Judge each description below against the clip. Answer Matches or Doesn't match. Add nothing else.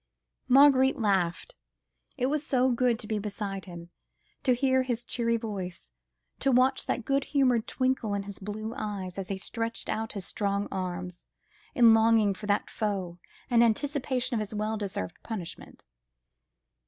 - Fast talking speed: Doesn't match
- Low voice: Doesn't match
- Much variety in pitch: Doesn't match